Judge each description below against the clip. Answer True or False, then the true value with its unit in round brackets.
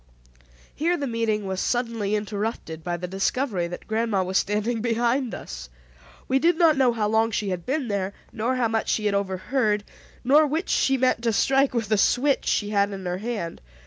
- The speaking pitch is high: True (220 Hz)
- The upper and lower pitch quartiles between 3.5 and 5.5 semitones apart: True (4.1 semitones)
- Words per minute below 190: False (195 wpm)